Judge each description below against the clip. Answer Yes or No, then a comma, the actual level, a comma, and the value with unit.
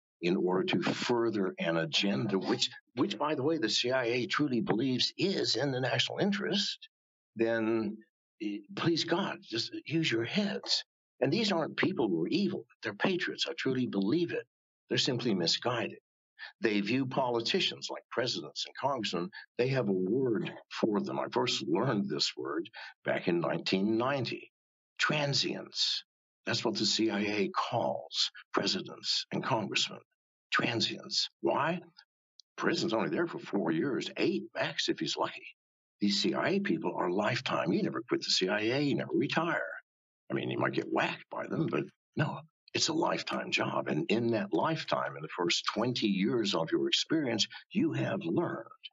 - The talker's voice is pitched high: No, low, 125 Hz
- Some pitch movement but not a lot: No, wide, 7.6 semitones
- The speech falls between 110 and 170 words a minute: Yes, average, 160 wpm